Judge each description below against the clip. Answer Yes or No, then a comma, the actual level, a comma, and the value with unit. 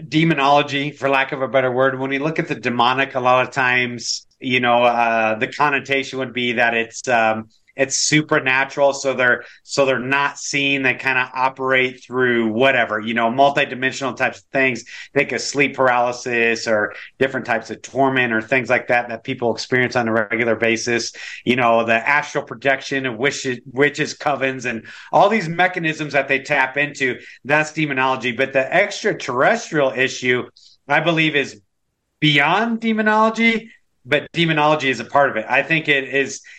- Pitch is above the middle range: No, low, 135 Hz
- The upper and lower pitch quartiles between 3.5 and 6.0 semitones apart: No, average, 2.9 semitones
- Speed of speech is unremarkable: Yes, average, 175 wpm